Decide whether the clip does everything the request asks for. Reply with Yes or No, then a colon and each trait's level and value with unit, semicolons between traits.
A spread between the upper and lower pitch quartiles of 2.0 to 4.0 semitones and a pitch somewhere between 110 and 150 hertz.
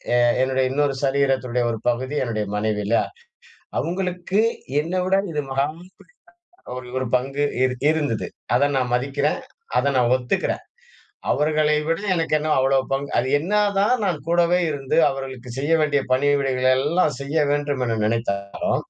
Yes: average, 3.3 semitones; medium, 140 Hz